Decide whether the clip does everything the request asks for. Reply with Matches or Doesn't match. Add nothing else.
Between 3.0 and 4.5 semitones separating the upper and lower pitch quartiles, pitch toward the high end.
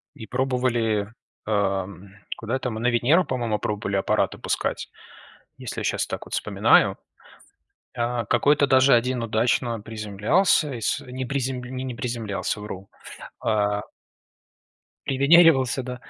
Doesn't match